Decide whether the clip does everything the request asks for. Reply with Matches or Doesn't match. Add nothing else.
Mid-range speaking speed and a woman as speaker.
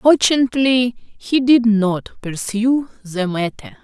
Doesn't match